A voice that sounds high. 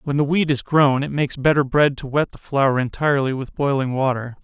No: medium, 140 Hz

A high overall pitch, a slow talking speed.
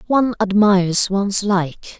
Yes: high, 200 Hz; slow, 120 wpm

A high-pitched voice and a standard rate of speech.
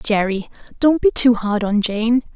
Yes: high, 225 Hz; average, 180 wpm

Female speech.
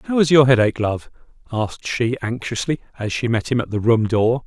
No: male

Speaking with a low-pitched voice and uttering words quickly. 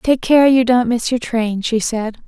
No: high, 240 Hz; fast, 235 wpm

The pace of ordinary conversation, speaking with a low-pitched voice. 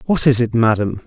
No: fast, 225 wpm; low, 120 Hz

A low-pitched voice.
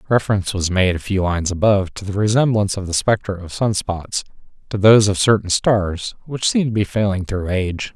Yes: low, 100 Hz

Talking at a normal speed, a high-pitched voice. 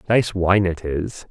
No: average, 185 wpm; very low, 95 Hz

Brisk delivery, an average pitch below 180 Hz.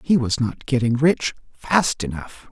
No: average, 165 wpm; low, 135 Hz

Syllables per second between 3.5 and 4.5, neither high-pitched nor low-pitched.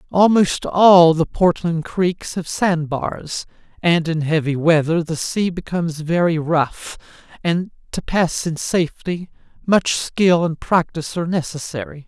Yes: 4.1 syllables/s; medium, 170 Hz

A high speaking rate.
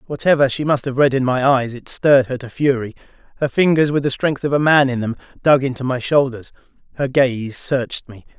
Yes: fast, 220 wpm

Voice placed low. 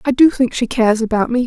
No: high, 240 Hz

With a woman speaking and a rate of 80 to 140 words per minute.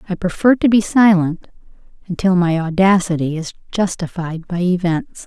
Yes: female; slow, 135 wpm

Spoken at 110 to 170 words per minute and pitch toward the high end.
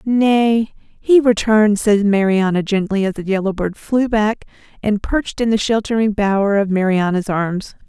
Yes: average, 160 wpm; high, 210 Hz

